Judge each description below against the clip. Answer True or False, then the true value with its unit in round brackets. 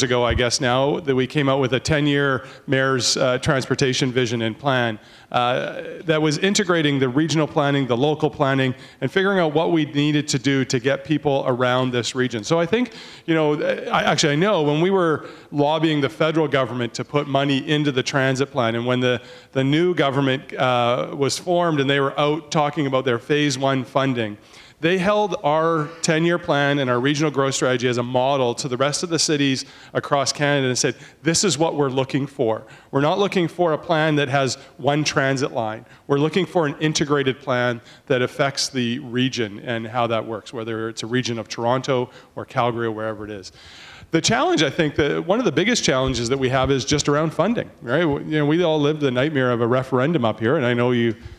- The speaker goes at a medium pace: False (220 wpm)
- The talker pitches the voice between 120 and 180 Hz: True (140 Hz)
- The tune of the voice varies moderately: True (3.5 semitones)